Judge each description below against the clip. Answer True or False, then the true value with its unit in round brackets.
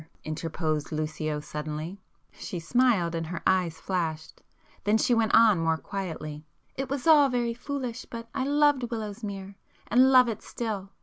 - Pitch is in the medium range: False (200 Hz)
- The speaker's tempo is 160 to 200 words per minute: False (145 wpm)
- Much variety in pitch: True (6.9 semitones)